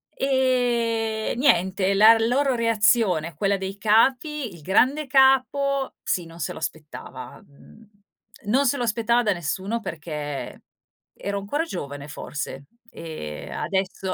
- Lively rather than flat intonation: Yes, wide, 6.5 semitones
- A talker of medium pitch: No, high, 215 Hz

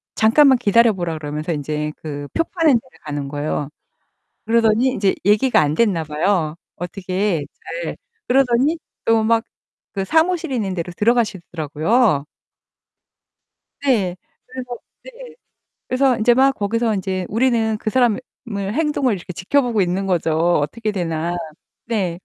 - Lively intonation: Yes, wide, 6.2 semitones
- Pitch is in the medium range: No, high, 210 Hz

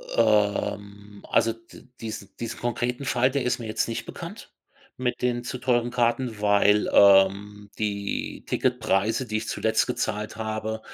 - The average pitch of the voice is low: Yes, low, 110 Hz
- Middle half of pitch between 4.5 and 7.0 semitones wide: No, average, 2.7 semitones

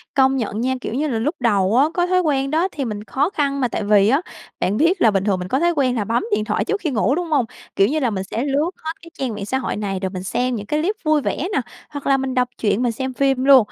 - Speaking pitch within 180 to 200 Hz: No, very high, 260 Hz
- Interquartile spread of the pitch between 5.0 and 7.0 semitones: Yes, wide, 5.4 semitones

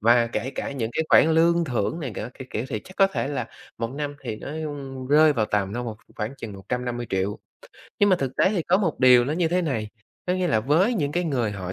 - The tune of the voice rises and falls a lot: Yes, wide, 6.3 semitones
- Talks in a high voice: No, low, 135 Hz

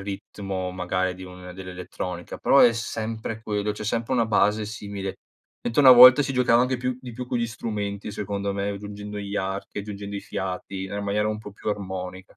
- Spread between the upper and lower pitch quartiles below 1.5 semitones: No, average, 2.8 semitones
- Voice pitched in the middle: No, low, 105 Hz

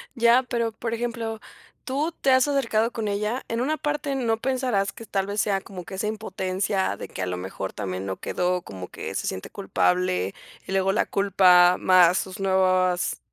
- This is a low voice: No, high, 200 Hz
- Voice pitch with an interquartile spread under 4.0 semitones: No, average, 4.3 semitones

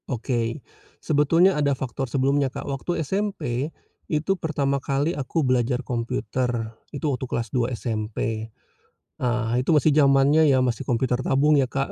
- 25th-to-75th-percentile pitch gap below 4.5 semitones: Yes, average, 3.1 semitones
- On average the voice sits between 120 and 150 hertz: Yes, low, 135 Hz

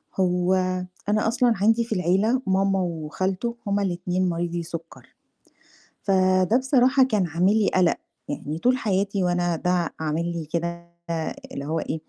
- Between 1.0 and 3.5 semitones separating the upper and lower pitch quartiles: Yes, average, 3.0 semitones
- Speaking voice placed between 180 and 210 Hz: Yes, medium, 185 Hz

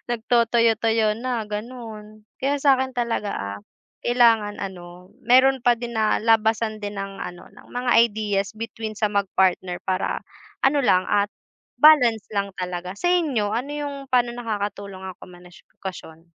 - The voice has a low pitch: No, high, 220 Hz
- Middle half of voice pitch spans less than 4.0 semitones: Yes, average, 3.5 semitones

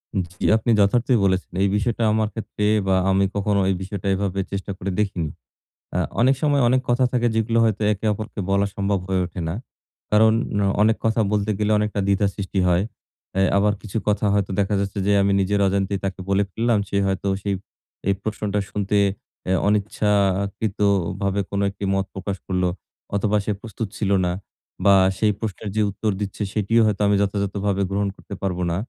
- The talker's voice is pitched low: Yes, low, 100 Hz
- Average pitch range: No, narrow, 1.6 semitones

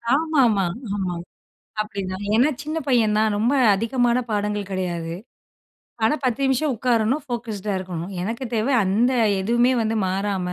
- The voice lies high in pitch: Yes, high, 220 Hz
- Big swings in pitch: No, average, 4.0 semitones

